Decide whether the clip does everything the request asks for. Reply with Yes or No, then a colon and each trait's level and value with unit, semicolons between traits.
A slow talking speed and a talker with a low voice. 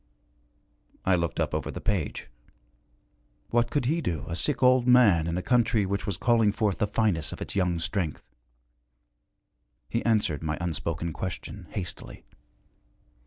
No: average, 150 wpm; very low, 95 Hz